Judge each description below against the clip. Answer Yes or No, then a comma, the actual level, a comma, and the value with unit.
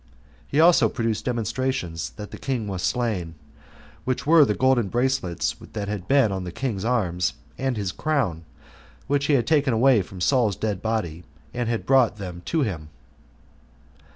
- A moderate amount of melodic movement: No, wide, 5.8 semitones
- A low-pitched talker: Yes, low, 115 Hz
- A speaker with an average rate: Yes, average, 165 wpm